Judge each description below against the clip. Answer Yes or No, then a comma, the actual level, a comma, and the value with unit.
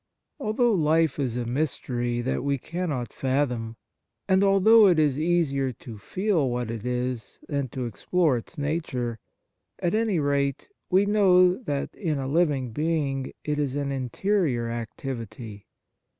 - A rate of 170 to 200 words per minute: No, average, 145 wpm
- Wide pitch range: Yes, wide, 5.9 semitones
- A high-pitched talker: No, medium, 140 Hz